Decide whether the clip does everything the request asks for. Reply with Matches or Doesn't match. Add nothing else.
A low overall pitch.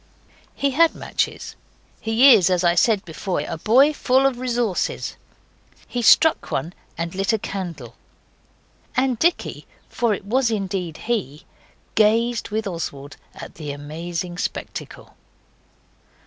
Doesn't match